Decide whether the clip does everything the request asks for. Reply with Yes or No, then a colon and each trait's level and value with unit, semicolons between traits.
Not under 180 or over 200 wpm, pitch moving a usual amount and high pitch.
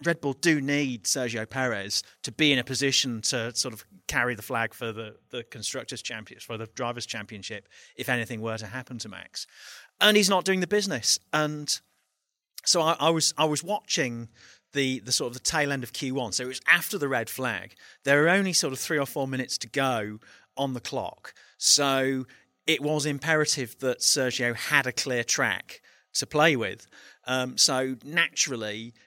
No: average, 190 wpm; average, 3.7 semitones; low, 130 Hz